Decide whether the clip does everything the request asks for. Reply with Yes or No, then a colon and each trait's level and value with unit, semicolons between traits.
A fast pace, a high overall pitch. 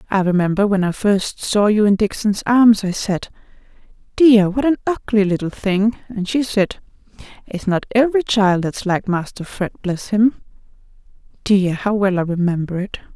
No: average, 170 wpm; high, 205 Hz